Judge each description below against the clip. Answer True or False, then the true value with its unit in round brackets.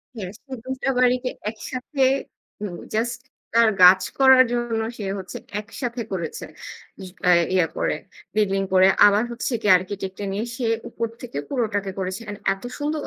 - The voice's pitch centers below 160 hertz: False (220 Hz)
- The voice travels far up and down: False (4.5 semitones)